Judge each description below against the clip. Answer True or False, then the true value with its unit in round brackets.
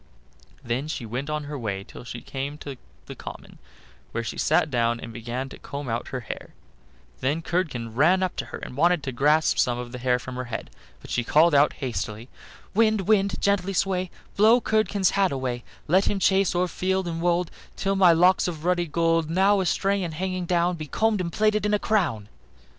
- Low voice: False (165 Hz)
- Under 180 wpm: False (205 wpm)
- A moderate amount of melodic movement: False (6.8 semitones)